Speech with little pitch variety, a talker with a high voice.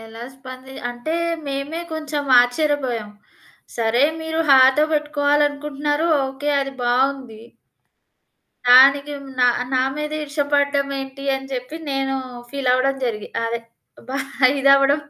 Yes: narrow, 2.2 semitones; very high, 275 Hz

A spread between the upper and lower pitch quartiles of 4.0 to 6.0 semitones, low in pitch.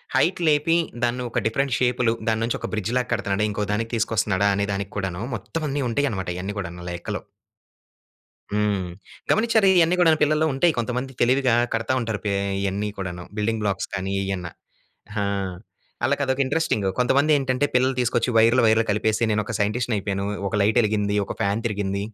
Yes: average, 4.3 semitones; low, 115 Hz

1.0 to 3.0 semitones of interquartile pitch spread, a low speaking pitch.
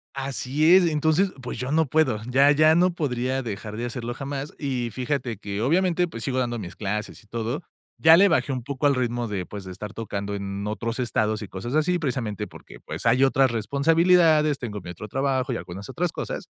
No: wide, 5.5 semitones; low, 130 Hz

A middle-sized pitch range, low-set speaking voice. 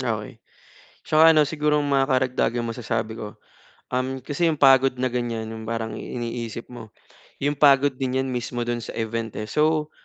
Yes: average, 3.5 semitones; low, 125 Hz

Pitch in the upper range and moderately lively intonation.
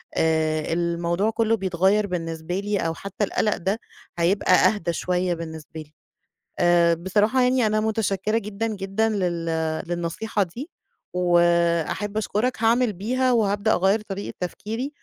Yes: high, 195 Hz; average, 4.1 semitones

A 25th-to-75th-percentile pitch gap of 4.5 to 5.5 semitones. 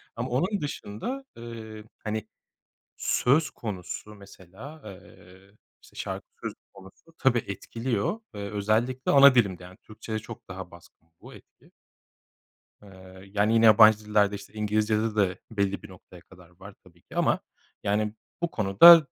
No: average, 3.0 semitones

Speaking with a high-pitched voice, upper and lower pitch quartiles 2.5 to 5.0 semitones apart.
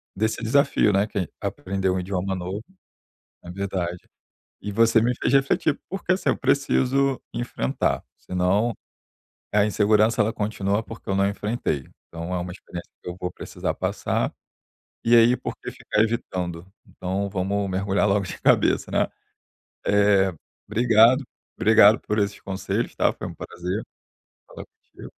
No: low, 100 Hz; average, 3.4 semitones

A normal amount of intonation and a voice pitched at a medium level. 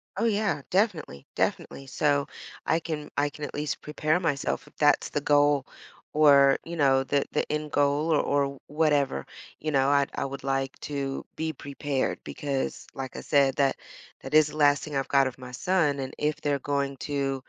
No: narrow, 1.7 semitones; medium, 145 Hz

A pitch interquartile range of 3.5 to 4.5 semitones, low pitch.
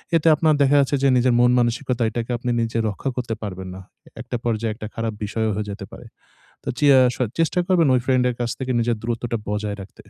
No: average, 2.7 semitones; low, 120 Hz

